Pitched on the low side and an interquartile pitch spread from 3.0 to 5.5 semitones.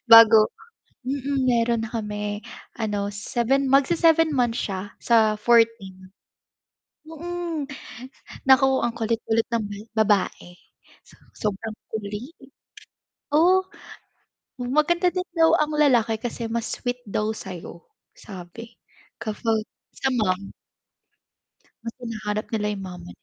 No: high, 230 Hz; average, 4.2 semitones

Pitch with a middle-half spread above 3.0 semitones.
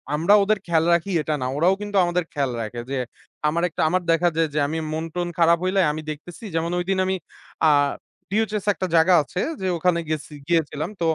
No: average, 2.7 semitones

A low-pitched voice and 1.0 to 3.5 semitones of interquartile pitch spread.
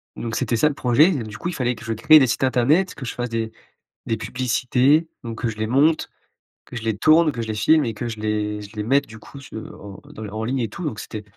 No: low, 120 Hz; average, 4.1 semitones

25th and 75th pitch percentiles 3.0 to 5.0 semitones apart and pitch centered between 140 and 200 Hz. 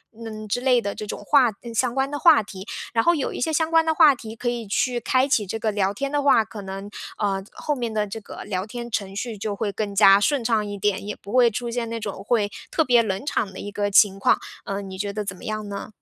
No: average, 3.4 semitones; high, 220 Hz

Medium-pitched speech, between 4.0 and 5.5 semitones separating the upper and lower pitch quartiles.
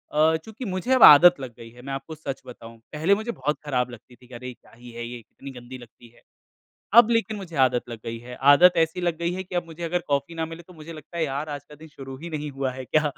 Yes: medium, 150 Hz; average, 5.1 semitones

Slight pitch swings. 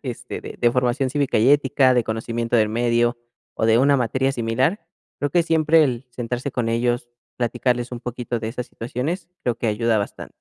Yes: narrow, 2.2 semitones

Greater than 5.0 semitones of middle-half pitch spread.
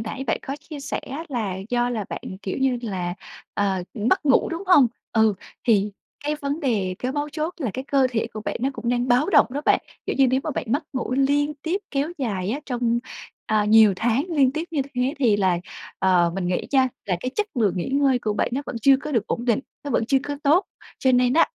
No: average, 4.5 semitones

